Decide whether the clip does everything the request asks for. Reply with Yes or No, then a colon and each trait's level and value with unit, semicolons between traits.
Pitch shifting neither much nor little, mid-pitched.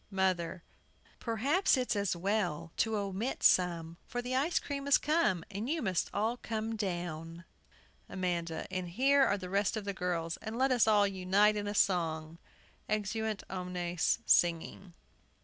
No: average, 4.2 semitones; high, 195 Hz